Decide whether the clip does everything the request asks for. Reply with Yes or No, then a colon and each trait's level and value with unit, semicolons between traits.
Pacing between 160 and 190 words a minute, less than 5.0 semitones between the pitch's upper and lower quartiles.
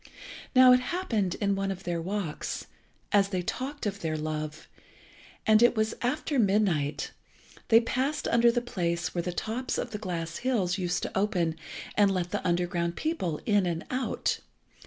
No: average, 170 wpm; wide, 5.4 semitones